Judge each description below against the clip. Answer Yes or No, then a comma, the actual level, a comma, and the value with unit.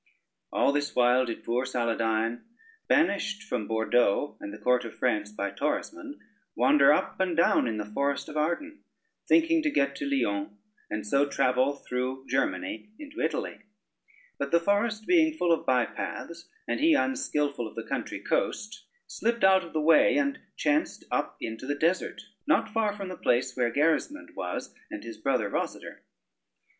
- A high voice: No, medium, 140 Hz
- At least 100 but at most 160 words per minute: No, average, 170 wpm